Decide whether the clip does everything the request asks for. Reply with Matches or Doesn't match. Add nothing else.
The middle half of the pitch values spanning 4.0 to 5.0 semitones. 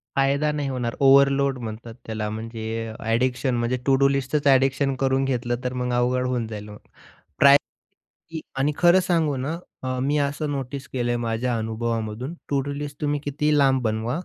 Doesn't match